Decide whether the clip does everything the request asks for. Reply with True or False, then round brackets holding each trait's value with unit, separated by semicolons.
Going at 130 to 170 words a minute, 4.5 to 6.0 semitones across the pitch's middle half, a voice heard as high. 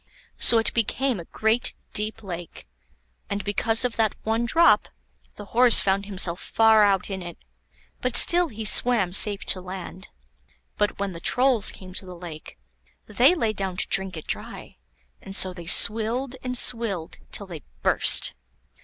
False (165 wpm; 3.6 semitones; 205 Hz)